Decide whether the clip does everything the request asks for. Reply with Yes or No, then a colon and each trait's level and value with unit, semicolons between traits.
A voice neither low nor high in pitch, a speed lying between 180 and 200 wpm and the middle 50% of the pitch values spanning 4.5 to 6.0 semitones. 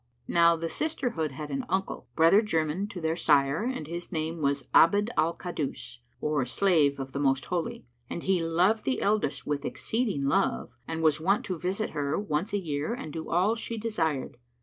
Yes: medium, 165 Hz; average, 190 wpm; average, 5.0 semitones